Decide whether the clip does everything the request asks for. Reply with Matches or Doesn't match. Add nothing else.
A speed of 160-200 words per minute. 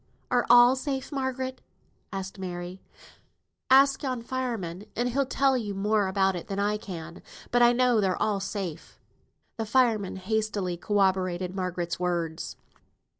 Doesn't match